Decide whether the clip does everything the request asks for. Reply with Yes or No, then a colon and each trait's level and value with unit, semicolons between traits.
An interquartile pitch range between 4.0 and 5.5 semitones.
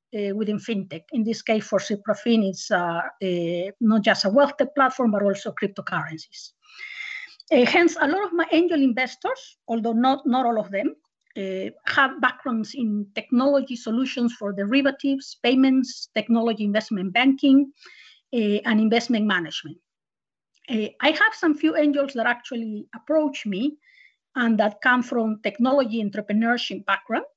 Yes: average, 4.8 semitones